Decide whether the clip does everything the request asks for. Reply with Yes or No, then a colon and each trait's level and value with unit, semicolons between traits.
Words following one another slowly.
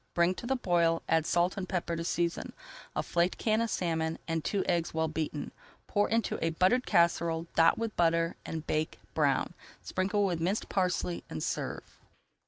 No: average, 190 wpm